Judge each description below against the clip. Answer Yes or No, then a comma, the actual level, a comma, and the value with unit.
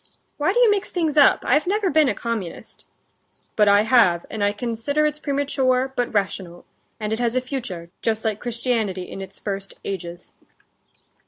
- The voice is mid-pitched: No, high, 230 Hz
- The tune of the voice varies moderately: No, wide, 5.9 semitones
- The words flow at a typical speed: Yes, average, 175 wpm